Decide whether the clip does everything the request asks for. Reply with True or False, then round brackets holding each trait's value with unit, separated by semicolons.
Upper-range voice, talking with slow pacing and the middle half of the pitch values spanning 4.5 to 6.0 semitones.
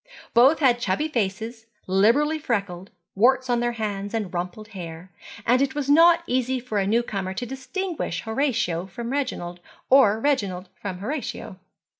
False (230 Hz; 155 wpm; 5.1 semitones)